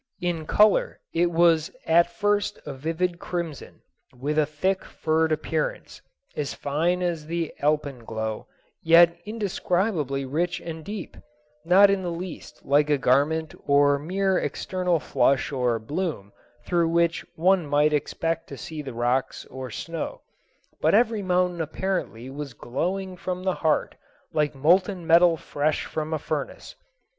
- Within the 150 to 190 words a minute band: No, average, 140 wpm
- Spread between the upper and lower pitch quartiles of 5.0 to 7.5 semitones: No, average, 3.8 semitones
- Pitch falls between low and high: Yes, medium, 165 Hz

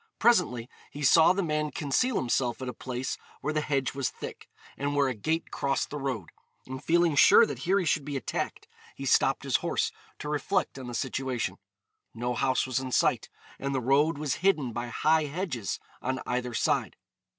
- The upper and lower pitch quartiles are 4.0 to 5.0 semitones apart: No, average, 3.5 semitones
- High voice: No, medium, 140 Hz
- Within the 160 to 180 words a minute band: No, average, 195 wpm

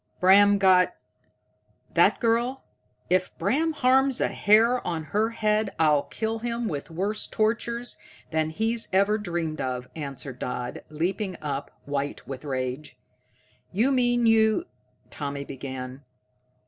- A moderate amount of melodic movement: No, wide, 7.6 semitones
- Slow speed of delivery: Yes, slow, 130 wpm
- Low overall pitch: No, high, 195 Hz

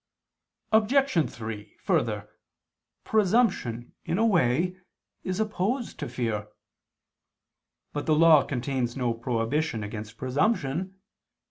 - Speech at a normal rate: No, slow, 100 wpm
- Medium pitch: Yes, medium, 145 Hz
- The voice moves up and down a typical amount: No, wide, 8.2 semitones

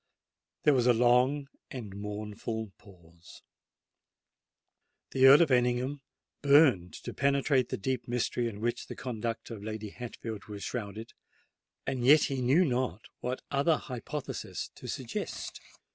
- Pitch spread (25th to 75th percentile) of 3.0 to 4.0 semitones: Yes, average, 3.6 semitones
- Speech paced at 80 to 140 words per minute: Yes, slow, 135 wpm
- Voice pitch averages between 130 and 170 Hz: No, low, 120 Hz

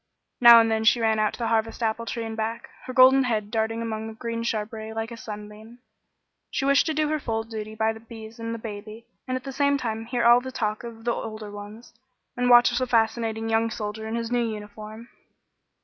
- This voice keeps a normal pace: No, fast, 225 wpm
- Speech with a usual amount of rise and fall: No, narrow, 1.4 semitones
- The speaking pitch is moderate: No, high, 225 Hz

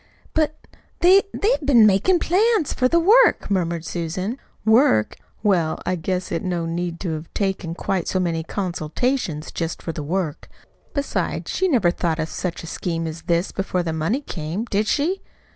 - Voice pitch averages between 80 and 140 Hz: No, medium, 185 Hz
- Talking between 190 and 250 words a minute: No, average, 175 wpm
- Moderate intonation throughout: No, wide, 7.4 semitones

